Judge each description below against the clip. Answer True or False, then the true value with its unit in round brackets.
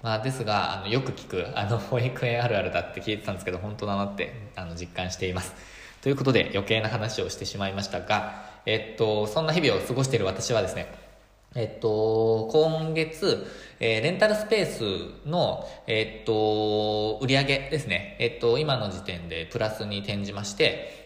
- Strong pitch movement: False (3.8 semitones)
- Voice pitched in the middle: False (110 Hz)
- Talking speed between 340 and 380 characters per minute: True (365 characters per minute)